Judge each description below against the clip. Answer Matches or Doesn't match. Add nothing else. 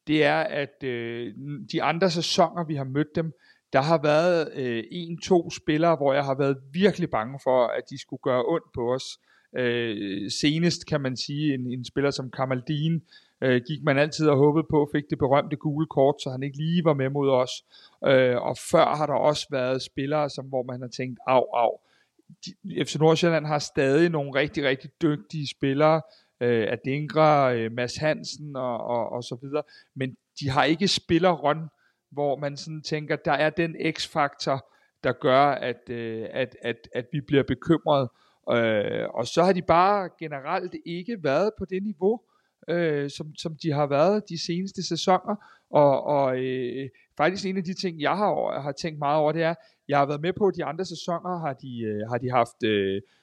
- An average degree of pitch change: Matches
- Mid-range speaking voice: Matches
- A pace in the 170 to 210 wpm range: Matches